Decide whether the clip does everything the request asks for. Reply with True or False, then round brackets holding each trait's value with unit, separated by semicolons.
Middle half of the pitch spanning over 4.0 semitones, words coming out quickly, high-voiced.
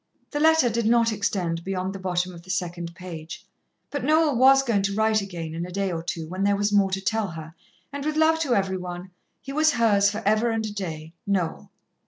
True (4.6 semitones; 230 wpm; 200 Hz)